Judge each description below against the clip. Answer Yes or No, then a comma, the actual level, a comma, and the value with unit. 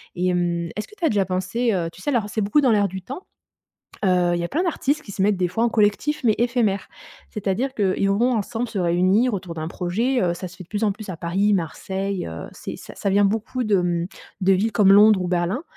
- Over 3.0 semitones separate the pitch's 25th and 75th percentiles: Yes, average, 3.7 semitones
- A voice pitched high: Yes, high, 200 Hz